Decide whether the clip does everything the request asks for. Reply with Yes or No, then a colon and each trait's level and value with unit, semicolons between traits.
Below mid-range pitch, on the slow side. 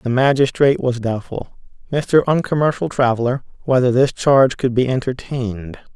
Yes: low, 130 Hz; slow, 130 wpm